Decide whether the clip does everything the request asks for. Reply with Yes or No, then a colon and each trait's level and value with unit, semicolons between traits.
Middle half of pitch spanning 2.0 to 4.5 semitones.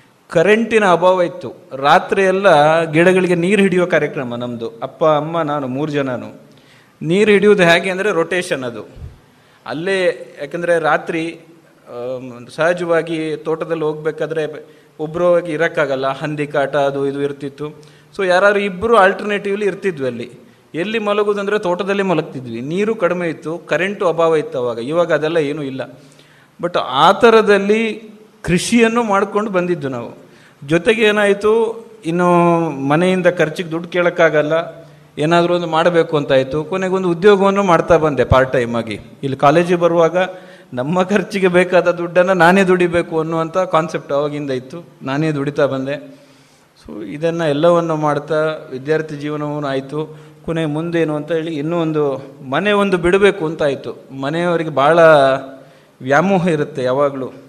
Yes: average, 3.7 semitones